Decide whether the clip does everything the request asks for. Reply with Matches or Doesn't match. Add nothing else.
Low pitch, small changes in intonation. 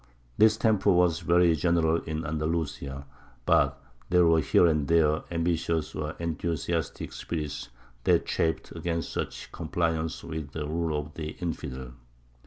Matches